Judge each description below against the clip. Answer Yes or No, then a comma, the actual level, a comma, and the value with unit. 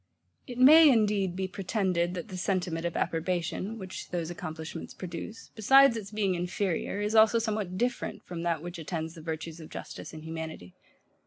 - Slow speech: No, average, 170 wpm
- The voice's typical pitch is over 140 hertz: Yes, medium, 185 Hz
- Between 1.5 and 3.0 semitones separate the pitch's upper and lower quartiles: No, average, 4.2 semitones